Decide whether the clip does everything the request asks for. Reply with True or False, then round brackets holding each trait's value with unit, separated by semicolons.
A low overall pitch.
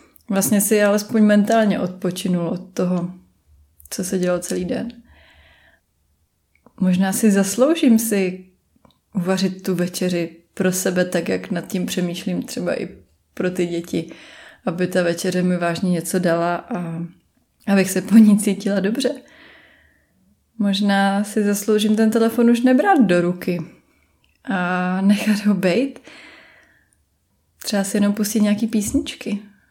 False (190 Hz)